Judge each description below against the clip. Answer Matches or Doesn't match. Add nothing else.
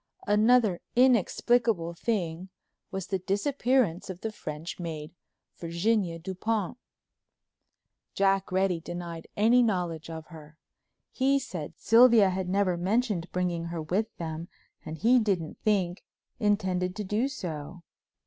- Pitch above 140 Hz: Matches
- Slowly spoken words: Matches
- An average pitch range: Matches